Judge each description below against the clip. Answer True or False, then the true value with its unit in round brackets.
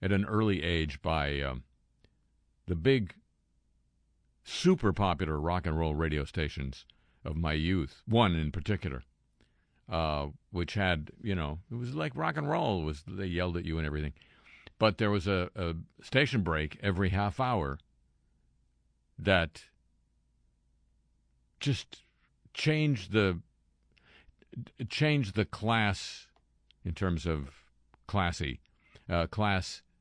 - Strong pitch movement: True (6.2 semitones)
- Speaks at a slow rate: True (125 wpm)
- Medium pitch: False (85 Hz)